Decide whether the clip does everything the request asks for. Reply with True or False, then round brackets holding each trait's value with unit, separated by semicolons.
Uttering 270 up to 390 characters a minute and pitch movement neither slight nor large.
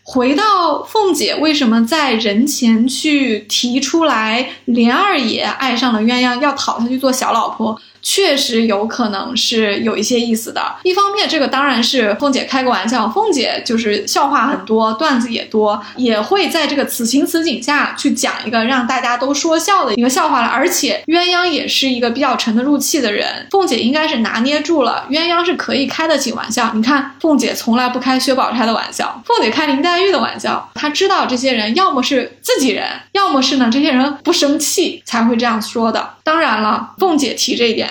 True (300 characters per minute; 4.8 semitones)